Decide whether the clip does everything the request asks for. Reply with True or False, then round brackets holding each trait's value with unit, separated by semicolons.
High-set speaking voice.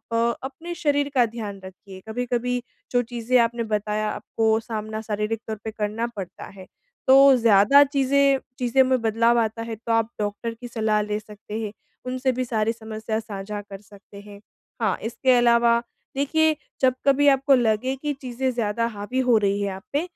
True (230 Hz)